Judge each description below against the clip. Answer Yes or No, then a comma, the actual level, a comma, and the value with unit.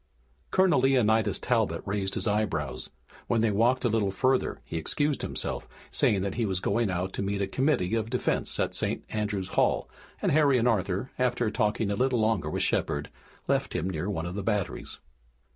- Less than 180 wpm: No, average, 185 wpm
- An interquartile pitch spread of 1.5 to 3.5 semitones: No, average, 4.2 semitones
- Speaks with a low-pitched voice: Yes, low, 105 Hz